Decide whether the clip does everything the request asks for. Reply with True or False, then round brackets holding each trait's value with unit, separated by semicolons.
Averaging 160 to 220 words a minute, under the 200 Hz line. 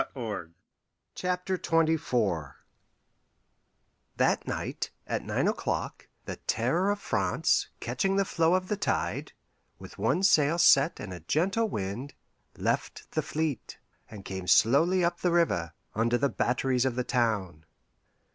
False (135 wpm; 140 Hz)